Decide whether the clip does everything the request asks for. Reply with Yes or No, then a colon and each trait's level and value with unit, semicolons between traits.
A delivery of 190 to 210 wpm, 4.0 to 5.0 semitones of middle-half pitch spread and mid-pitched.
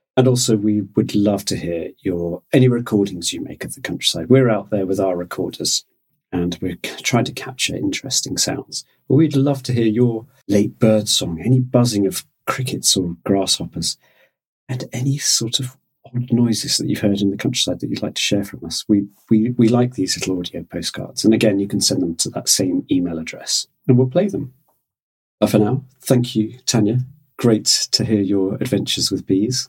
No: average, 200 wpm; average, 4.4 semitones; low, 110 Hz